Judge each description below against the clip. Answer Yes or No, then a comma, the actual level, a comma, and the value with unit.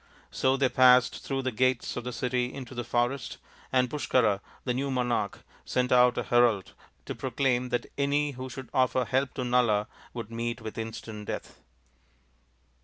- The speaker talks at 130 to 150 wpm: No, average, 170 wpm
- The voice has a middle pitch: No, low, 125 Hz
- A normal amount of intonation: No, narrow, 1.6 semitones